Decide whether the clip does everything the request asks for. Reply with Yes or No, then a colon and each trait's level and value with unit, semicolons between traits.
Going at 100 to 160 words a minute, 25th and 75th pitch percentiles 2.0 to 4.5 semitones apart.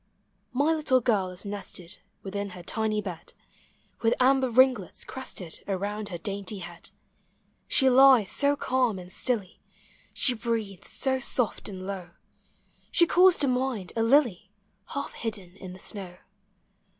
No: average, 140 wpm; wide, 5.5 semitones